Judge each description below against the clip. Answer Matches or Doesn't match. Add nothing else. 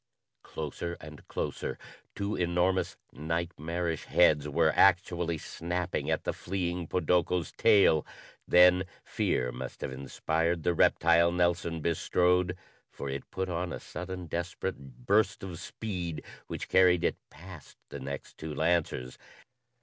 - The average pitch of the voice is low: Matches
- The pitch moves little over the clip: Matches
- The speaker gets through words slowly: Matches